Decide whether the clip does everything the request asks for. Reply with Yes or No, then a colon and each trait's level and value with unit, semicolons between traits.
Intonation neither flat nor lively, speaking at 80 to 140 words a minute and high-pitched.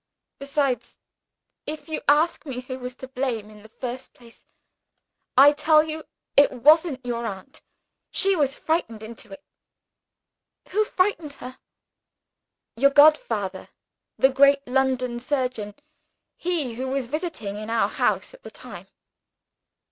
Yes: average, 4.1 semitones; slow, 135 wpm; very high, 265 Hz